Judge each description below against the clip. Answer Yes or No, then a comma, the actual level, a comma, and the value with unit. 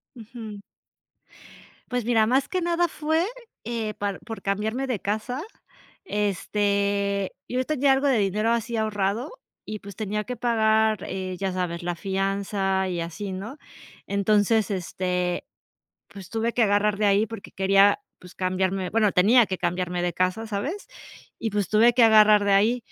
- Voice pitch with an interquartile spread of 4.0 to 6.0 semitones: No, average, 2.9 semitones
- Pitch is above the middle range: Yes, high, 210 Hz